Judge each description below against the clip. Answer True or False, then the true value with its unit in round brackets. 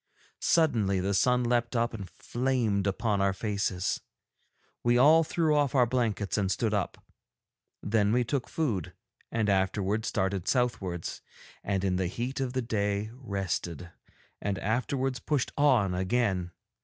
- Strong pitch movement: False (4.2 semitones)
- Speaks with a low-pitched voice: True (110 Hz)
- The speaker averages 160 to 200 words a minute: False (145 wpm)